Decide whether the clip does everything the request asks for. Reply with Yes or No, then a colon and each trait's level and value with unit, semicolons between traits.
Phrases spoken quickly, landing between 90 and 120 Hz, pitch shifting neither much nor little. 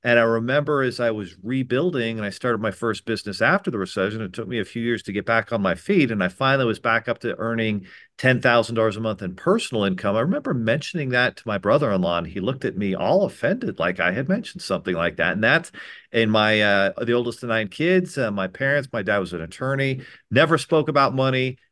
Yes: fast, 235 wpm; low, 115 Hz; average, 3.4 semitones